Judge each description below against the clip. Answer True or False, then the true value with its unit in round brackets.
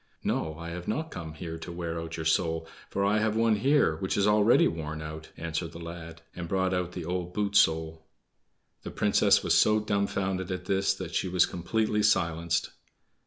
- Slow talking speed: False (195 wpm)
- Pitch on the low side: True (90 Hz)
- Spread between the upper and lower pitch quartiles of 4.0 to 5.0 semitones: False (3.5 semitones)